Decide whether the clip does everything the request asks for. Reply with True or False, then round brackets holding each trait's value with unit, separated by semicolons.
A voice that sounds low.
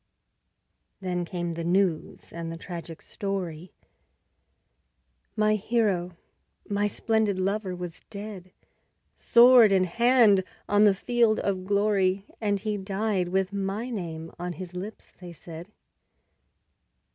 False (195 Hz)